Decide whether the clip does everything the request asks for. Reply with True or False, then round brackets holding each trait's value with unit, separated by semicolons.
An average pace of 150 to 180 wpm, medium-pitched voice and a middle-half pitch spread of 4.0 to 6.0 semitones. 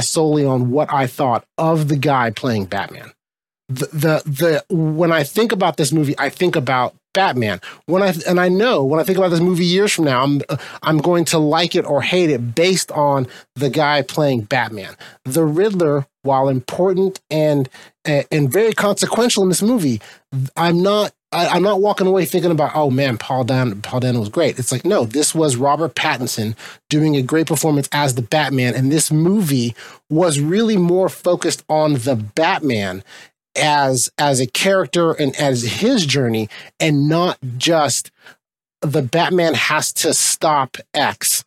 True (170 wpm; 150 Hz; 4.3 semitones)